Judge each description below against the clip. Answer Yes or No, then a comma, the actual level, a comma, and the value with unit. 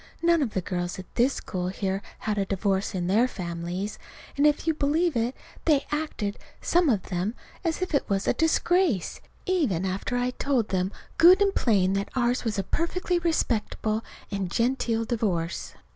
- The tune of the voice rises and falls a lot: Yes, wide, 7.6 semitones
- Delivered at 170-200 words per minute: Yes, average, 175 wpm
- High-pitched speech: Yes, high, 225 Hz